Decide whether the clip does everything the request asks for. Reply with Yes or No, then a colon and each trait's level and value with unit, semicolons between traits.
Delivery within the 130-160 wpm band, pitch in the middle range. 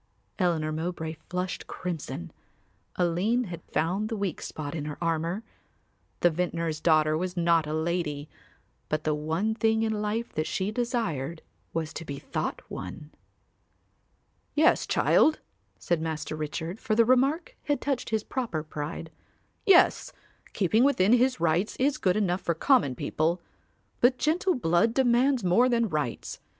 Yes: average, 145 wpm; medium, 175 Hz